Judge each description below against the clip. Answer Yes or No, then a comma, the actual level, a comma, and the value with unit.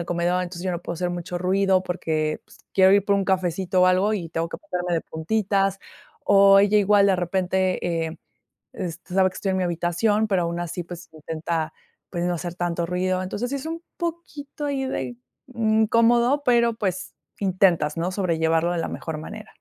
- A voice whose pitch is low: No, medium, 185 Hz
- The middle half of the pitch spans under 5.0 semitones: Yes, average, 2.8 semitones